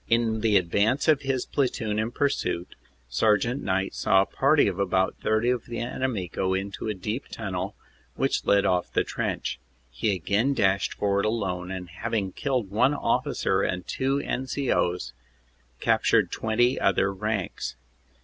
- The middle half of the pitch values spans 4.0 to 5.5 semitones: Yes, average, 4.3 semitones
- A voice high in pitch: No, low, 105 Hz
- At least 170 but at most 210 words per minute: No, average, 160 wpm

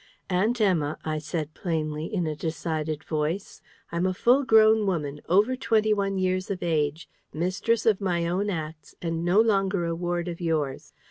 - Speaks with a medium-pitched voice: Yes, medium, 175 Hz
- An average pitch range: Yes, average, 4.1 semitones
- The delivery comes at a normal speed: Yes, average, 175 wpm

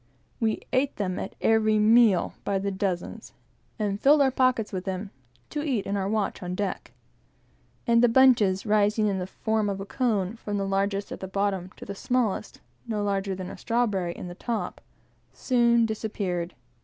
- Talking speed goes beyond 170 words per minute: Yes, average, 180 wpm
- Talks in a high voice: Yes, high, 205 Hz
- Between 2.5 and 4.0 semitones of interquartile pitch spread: Yes, average, 3.0 semitones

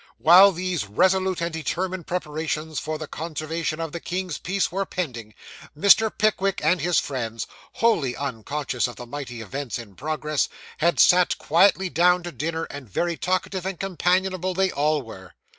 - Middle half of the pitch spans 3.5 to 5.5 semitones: Yes, average, 4.4 semitones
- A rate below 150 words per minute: No, average, 160 wpm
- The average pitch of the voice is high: No, medium, 165 Hz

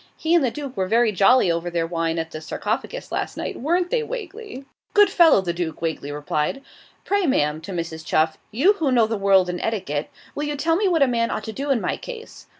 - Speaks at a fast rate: Yes, fast, 235 wpm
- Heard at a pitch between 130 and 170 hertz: No, high, 225 Hz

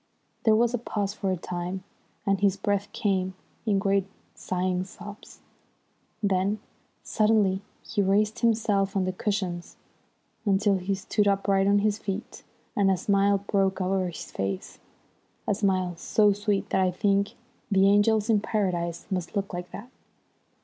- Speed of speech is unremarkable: Yes, average, 150 wpm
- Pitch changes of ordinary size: No, narrow, 1.7 semitones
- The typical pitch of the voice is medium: No, high, 195 Hz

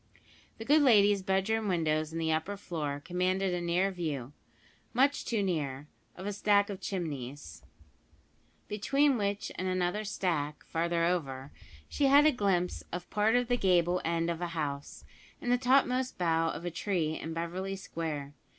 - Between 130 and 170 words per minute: Yes, average, 165 wpm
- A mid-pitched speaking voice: Yes, medium, 180 Hz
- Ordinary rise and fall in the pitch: Yes, average, 4.1 semitones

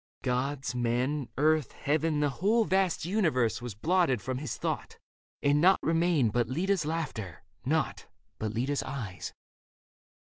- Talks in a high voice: No, medium, 145 Hz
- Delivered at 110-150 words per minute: Yes, slow, 135 wpm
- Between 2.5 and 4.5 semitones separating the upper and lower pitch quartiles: No, average, 4.9 semitones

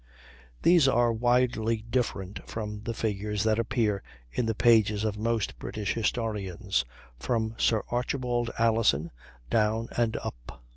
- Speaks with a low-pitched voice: Yes, low, 110 Hz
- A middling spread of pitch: No, narrow, 2.0 semitones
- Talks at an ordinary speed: No, slow, 130 wpm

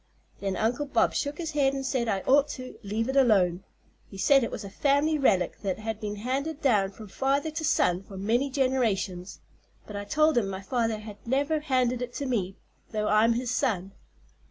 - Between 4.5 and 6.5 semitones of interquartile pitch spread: Yes, average, 5.2 semitones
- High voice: Yes, high, 235 Hz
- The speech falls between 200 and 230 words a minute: Yes, fast, 205 wpm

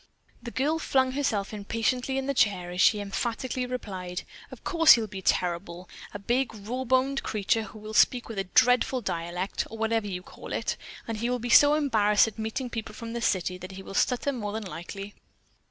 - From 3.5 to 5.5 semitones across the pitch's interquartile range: Yes, average, 4.1 semitones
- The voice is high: Yes, high, 225 Hz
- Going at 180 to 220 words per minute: Yes, average, 200 wpm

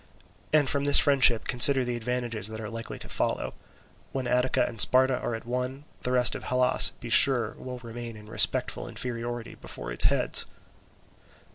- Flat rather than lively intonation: Yes, narrow, 1.8 semitones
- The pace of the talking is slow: No, average, 170 wpm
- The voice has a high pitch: No, low, 125 Hz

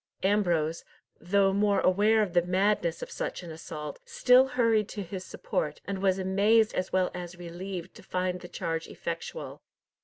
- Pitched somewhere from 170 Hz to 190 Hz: Yes, medium, 185 Hz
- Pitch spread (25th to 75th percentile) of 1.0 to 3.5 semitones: Yes, average, 2.8 semitones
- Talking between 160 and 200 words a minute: Yes, average, 165 wpm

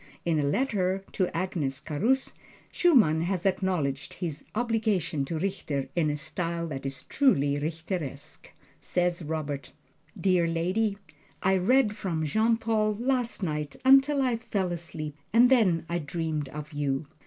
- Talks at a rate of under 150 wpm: Yes, average, 140 wpm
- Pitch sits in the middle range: Yes, medium, 175 Hz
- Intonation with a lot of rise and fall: Yes, wide, 5.9 semitones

